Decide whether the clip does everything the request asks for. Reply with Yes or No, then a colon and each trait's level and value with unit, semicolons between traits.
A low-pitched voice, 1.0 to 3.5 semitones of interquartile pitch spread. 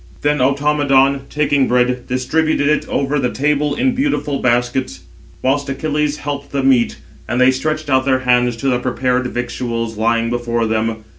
Yes: low, 130 Hz; average, 2.8 semitones